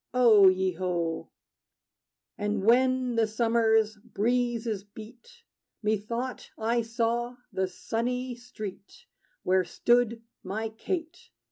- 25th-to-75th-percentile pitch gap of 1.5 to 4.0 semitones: Yes, average, 2.8 semitones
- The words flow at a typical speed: No, slow, 100 wpm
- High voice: Yes, high, 225 Hz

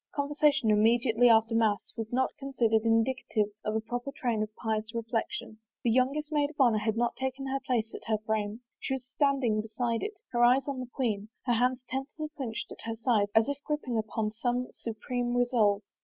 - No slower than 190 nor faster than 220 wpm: Yes, average, 200 wpm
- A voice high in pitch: Yes, high, 240 Hz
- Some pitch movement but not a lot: Yes, average, 3.2 semitones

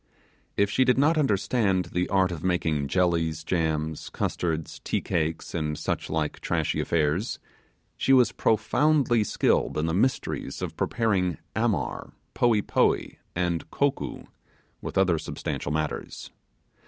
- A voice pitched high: No, very low, 90 Hz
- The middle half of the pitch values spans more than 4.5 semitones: Yes, wide, 5.6 semitones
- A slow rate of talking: Yes, slow, 130 wpm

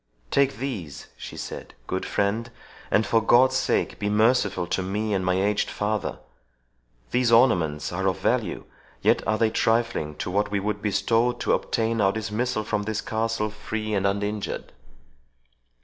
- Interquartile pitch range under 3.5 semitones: Yes, narrow, 2.4 semitones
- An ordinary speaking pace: Yes, average, 160 wpm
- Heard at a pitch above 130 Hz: No, low, 105 Hz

